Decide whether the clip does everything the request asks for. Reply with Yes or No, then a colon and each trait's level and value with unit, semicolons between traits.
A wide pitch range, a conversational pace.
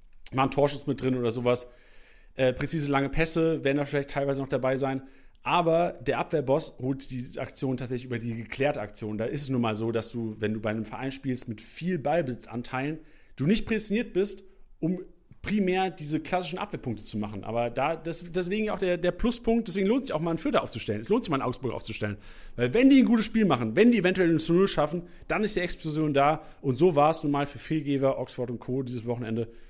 No: wide, 6.1 semitones; fast, 225 wpm